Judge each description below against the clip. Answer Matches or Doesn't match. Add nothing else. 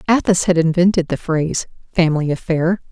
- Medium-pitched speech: Matches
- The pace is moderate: Matches